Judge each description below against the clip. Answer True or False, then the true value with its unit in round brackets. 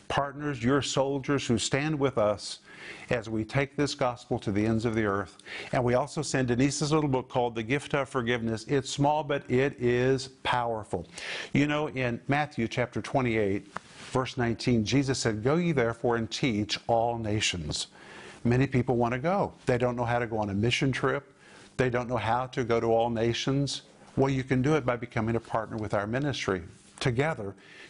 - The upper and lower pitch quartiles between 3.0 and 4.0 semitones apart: True (3.3 semitones)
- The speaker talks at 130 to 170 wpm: False (195 wpm)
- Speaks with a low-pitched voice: True (125 Hz)